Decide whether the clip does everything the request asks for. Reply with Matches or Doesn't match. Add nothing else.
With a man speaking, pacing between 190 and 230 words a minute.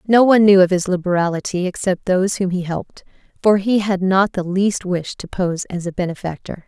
Doesn't match